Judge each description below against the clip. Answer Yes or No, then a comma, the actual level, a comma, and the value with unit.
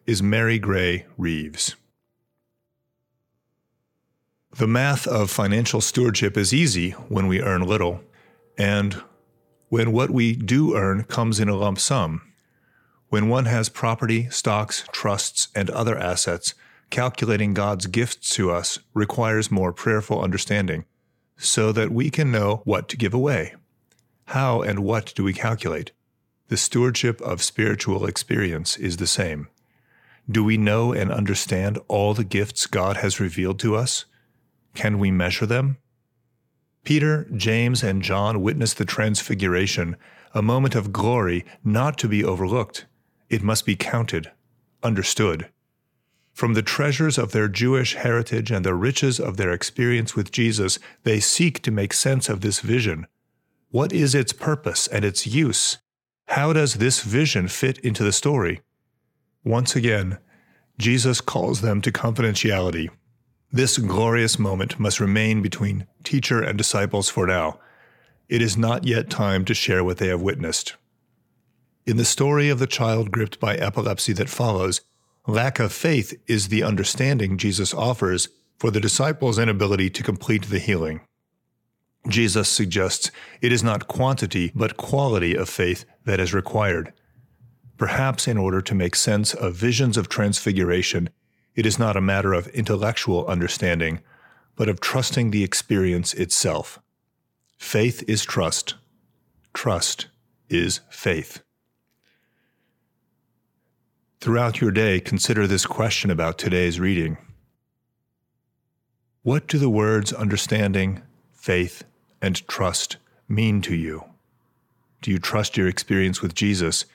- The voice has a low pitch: Yes, low, 110 Hz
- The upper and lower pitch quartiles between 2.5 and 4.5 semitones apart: Yes, average, 3.6 semitones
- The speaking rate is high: No, average, 140 wpm